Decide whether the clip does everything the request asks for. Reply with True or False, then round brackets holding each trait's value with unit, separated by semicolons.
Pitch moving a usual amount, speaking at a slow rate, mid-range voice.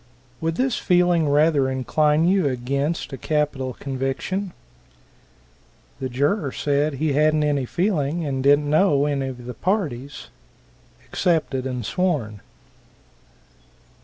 True (3.6 semitones; 115 wpm; 145 Hz)